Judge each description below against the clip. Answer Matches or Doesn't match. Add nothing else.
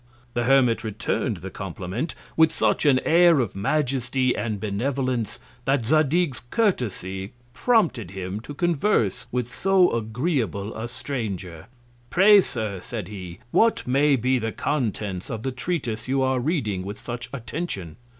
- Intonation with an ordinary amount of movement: Doesn't match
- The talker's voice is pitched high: Doesn't match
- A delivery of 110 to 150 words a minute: Matches